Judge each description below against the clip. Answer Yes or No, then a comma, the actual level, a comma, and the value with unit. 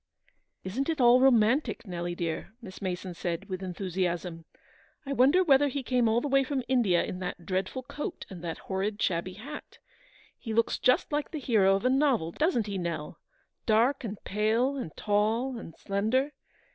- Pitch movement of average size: No, wide, 6.1 semitones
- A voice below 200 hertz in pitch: No, high, 220 Hz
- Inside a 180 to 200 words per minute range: Yes, average, 185 wpm